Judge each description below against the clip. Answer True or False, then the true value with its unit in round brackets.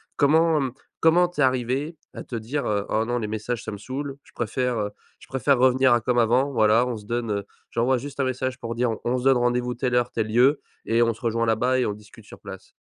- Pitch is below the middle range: True (125 Hz)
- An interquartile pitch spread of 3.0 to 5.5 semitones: False (2.4 semitones)